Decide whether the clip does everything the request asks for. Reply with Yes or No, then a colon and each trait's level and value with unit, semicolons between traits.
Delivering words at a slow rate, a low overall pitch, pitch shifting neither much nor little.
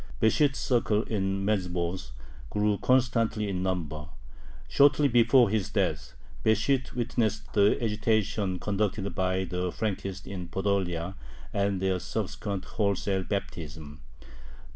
Yes: slow, 110 wpm; low, 100 Hz; average, 3.0 semitones